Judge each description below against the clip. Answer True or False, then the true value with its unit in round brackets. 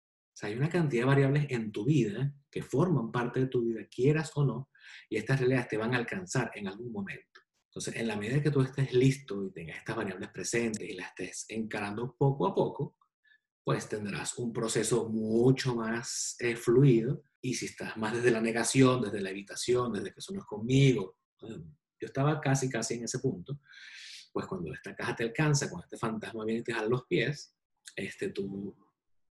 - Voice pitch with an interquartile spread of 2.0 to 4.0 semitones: True (3.5 semitones)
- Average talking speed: False (195 wpm)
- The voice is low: True (125 Hz)